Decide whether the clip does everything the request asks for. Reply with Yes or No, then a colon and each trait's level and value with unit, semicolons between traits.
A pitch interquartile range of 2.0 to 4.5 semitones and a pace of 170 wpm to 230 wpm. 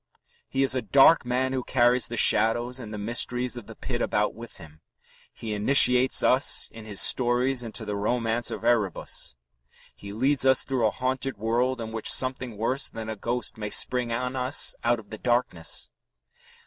Yes: narrow, 2.5 semitones; average, 185 wpm